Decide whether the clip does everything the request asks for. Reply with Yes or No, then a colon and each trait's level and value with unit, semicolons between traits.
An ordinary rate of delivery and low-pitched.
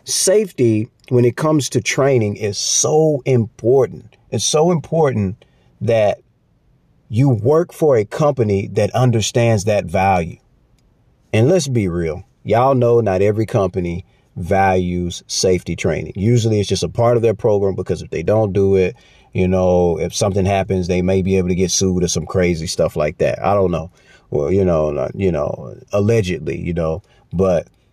Yes: average, 170 wpm; low, 105 Hz